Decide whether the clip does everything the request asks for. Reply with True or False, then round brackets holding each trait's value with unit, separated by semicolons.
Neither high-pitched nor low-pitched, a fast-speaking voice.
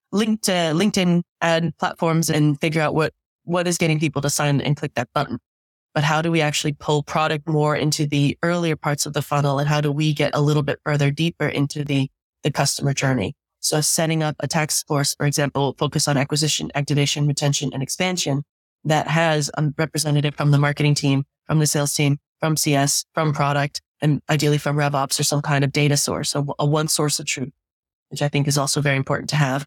True (150 Hz; 210 wpm)